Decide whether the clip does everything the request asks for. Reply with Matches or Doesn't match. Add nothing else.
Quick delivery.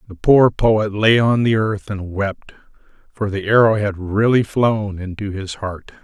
Doesn't match